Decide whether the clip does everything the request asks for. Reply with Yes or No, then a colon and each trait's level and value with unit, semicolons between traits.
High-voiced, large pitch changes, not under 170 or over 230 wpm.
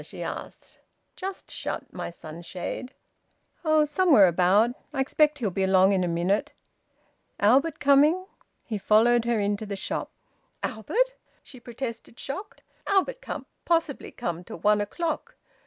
No: high, 235 Hz; wide, 7.3 semitones; average, 140 wpm